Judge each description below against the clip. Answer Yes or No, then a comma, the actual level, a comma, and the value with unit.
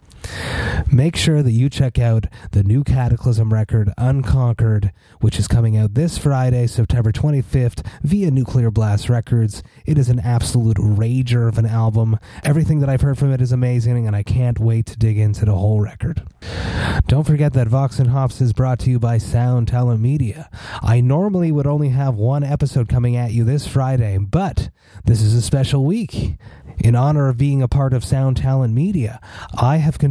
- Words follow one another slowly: No, average, 185 wpm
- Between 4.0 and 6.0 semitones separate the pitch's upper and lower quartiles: No, average, 3.3 semitones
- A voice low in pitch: Yes, low, 120 Hz